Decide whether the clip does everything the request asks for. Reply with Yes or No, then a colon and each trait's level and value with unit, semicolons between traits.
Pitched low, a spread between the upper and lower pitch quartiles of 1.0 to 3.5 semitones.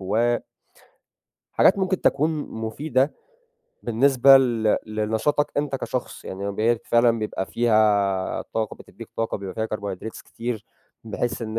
Yes: low, 115 Hz; average, 2.9 semitones